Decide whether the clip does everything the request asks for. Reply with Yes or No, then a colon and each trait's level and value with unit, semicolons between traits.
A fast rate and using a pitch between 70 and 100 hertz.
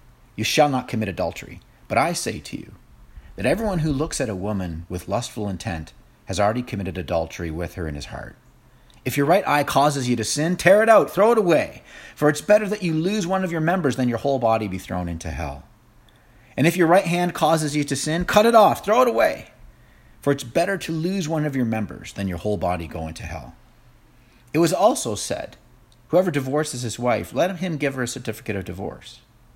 No: fast, 220 wpm; low, 125 Hz